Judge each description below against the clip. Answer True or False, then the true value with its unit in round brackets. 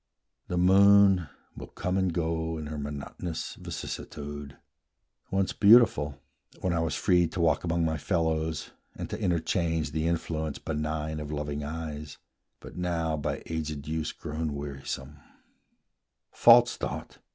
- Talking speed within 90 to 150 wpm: True (135 wpm)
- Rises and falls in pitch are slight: True (2.3 semitones)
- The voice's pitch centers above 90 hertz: False (80 Hz)